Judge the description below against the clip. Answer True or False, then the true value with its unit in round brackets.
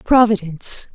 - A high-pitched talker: True (205 Hz)